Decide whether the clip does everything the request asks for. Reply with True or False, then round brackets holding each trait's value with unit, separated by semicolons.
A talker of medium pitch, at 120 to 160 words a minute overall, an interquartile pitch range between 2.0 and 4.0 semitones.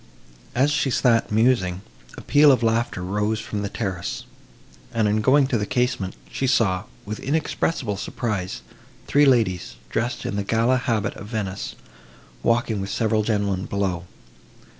False (110 Hz; 150 wpm; 3.7 semitones)